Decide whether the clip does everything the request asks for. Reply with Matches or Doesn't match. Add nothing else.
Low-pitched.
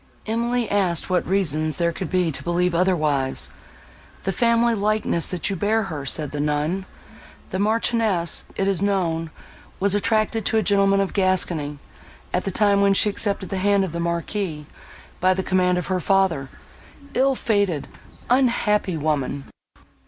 Doesn't match